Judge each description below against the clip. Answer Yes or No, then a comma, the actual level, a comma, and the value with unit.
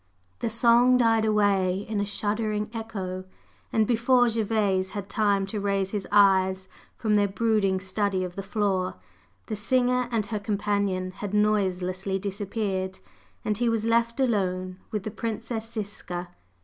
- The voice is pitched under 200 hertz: No, high, 205 Hz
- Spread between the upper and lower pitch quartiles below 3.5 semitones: Yes, average, 2.7 semitones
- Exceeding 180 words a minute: No, average, 150 wpm